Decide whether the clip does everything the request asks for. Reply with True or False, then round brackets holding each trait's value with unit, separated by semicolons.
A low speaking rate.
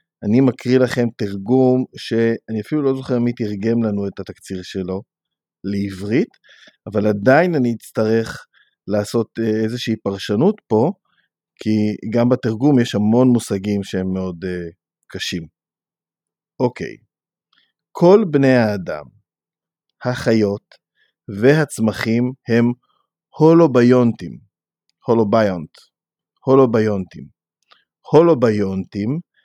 True (90 wpm)